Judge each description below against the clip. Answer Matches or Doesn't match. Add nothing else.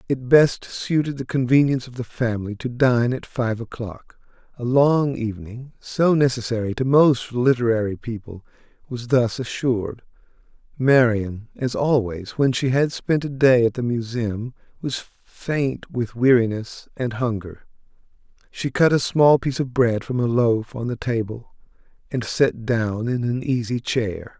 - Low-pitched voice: Matches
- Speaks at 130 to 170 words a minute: Matches